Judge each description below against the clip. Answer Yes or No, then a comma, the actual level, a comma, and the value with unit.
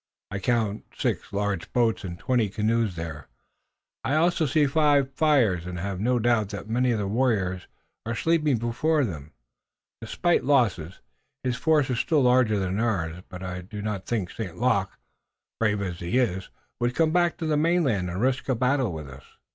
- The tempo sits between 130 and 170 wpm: No, average, 185 wpm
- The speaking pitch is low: Yes, low, 115 Hz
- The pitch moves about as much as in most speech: No, wide, 5.8 semitones